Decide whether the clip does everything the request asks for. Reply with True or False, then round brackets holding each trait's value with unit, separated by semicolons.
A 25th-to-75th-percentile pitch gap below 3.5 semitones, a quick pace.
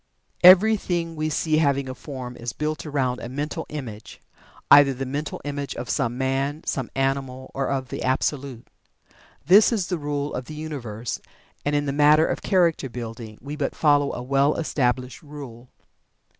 False (2.9 semitones; 170 wpm)